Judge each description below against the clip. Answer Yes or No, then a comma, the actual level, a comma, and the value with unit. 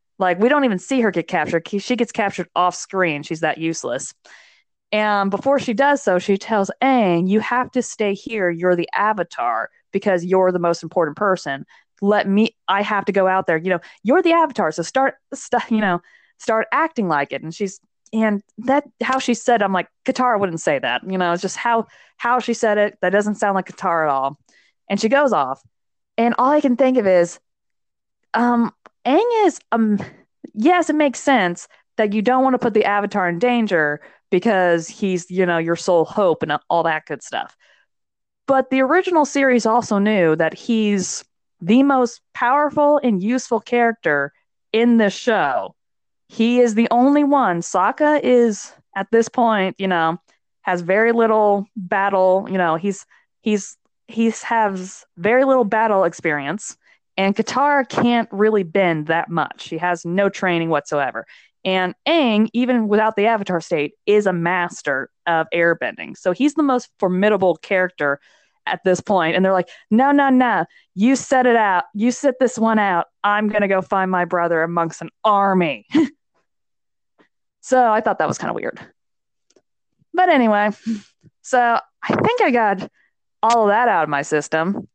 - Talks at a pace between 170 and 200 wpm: Yes, average, 180 wpm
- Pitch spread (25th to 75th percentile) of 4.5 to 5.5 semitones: Yes, average, 5.1 semitones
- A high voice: Yes, high, 210 Hz